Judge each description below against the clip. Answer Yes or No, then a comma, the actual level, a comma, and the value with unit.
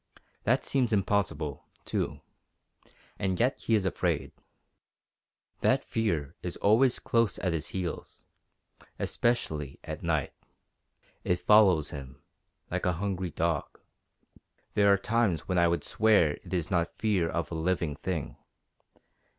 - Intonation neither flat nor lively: Yes, average, 4.2 semitones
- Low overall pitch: Yes, very low, 90 Hz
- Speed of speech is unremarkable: No, slow, 130 wpm